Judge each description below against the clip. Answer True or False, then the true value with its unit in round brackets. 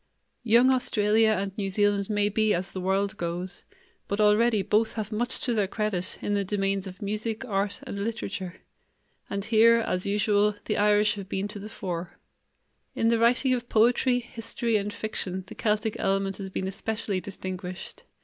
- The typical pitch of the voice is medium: False (205 Hz)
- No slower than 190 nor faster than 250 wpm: False (175 wpm)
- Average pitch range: False (2.3 semitones)